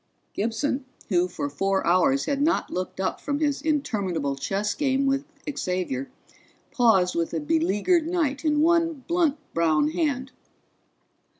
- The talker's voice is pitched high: Yes, high, 245 Hz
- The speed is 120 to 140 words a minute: Yes, slow, 135 wpm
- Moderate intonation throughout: No, wide, 8.4 semitones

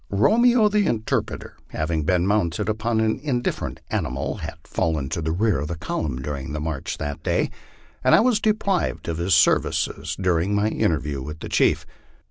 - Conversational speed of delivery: Yes, average, 175 wpm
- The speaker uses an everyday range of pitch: No, wide, 6.5 semitones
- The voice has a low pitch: Yes, very low, 90 Hz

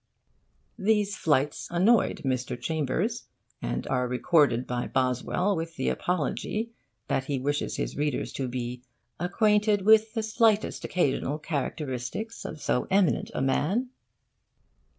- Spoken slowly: Yes, slow, 125 wpm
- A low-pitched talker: No, medium, 160 Hz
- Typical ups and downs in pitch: No, wide, 8.0 semitones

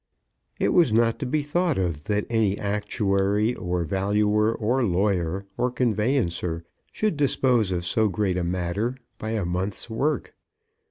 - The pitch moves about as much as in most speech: Yes, average, 4.4 semitones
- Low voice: Yes, low, 105 Hz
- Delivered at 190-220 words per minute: No, average, 150 wpm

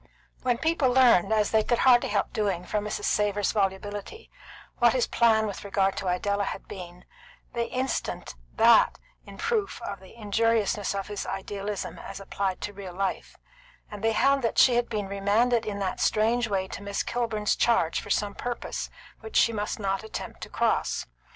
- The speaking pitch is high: Yes, high, 210 Hz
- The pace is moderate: Yes, average, 180 wpm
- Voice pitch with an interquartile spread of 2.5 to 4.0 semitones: Yes, average, 3.0 semitones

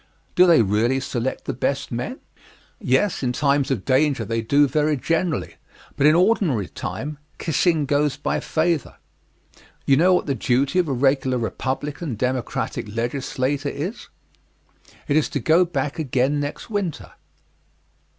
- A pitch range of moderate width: Yes, average, 3.4 semitones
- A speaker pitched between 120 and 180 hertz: Yes, medium, 140 Hz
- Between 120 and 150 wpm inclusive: Yes, average, 145 wpm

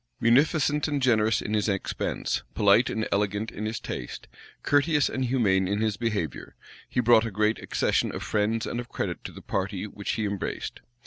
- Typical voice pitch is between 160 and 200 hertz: No, low, 110 Hz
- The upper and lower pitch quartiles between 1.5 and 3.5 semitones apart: Yes, average, 3.1 semitones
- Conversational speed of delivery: Yes, average, 185 wpm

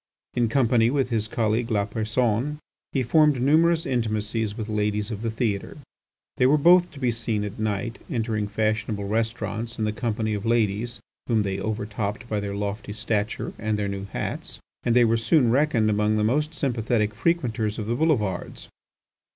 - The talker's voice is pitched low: Yes, low, 110 Hz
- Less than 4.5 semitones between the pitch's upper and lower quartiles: Yes, narrow, 2.5 semitones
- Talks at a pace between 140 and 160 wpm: No, average, 175 wpm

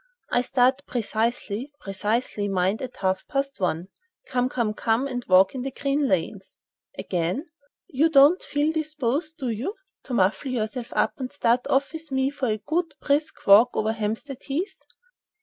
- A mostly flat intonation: No, average, 4.7 semitones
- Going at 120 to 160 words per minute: Yes, average, 155 wpm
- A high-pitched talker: Yes, very high, 250 Hz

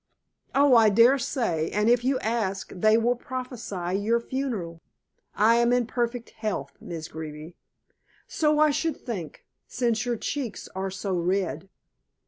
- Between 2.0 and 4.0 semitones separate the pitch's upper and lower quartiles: No, average, 4.6 semitones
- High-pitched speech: Yes, high, 225 Hz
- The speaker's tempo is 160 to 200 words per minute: No, average, 140 wpm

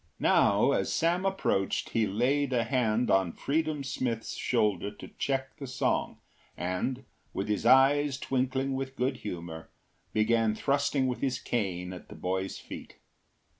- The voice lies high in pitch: No, low, 125 Hz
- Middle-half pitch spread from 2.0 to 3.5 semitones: No, average, 4.6 semitones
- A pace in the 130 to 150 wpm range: Yes, average, 145 wpm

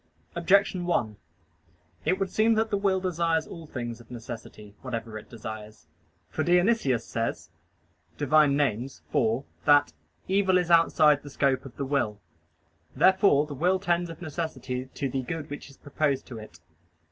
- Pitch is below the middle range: No, medium, 145 Hz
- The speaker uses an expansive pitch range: Yes, wide, 6.3 semitones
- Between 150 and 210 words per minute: Yes, average, 160 wpm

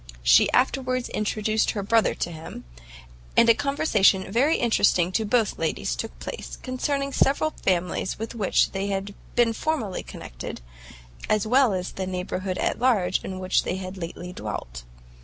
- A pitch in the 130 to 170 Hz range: No, high, 205 Hz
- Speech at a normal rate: Yes, average, 160 wpm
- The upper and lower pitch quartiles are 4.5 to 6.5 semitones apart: Yes, average, 5.0 semitones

